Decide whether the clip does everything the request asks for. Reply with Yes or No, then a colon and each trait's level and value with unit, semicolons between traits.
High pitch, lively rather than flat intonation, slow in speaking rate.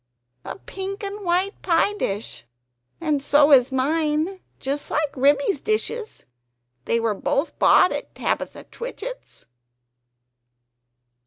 Yes: very high, 315 Hz; wide, 6.1 semitones; slow, 110 wpm